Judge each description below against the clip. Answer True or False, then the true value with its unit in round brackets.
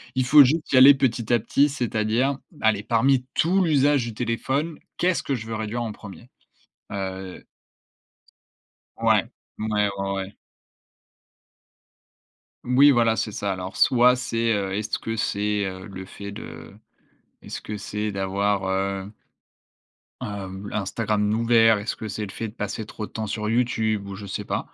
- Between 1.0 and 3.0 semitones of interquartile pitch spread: False (3.4 semitones)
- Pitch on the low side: True (110 Hz)